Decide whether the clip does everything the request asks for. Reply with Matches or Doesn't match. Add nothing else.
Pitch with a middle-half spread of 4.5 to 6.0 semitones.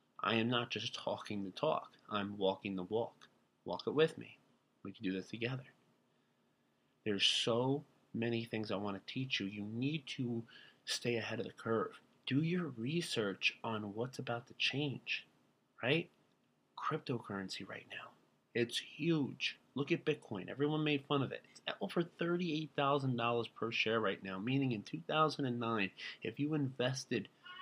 Matches